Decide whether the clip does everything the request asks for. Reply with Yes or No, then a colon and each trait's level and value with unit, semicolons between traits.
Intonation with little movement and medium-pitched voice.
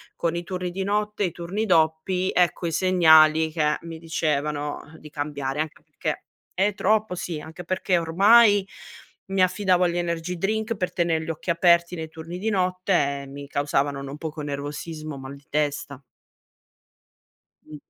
No: average, 3.4 semitones; medium, 165 Hz